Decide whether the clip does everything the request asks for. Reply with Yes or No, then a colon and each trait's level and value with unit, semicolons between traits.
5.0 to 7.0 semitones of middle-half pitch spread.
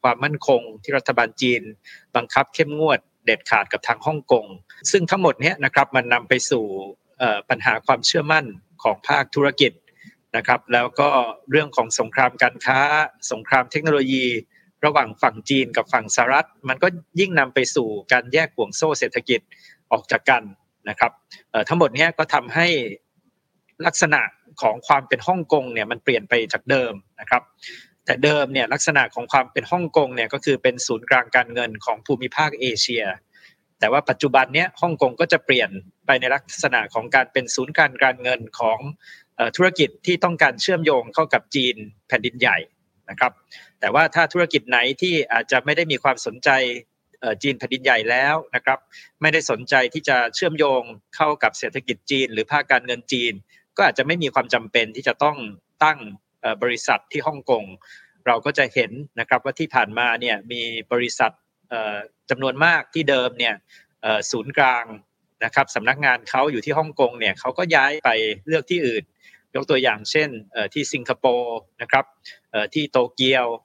No: average, 4.1 semitones